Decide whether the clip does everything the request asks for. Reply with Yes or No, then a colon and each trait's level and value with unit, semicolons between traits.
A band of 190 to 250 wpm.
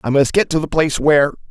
No: fast, 280 wpm